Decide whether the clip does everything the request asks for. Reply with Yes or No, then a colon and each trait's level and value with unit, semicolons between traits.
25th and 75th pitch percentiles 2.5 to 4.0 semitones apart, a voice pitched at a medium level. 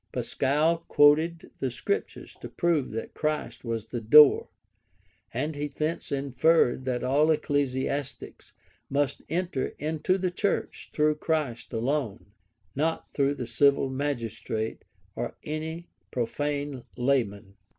Yes: average, 3.5 semitones; medium, 145 Hz